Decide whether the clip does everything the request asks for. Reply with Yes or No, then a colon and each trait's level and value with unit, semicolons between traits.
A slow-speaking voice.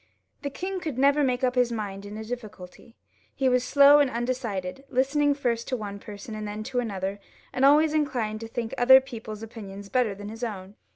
No: average, 195 wpm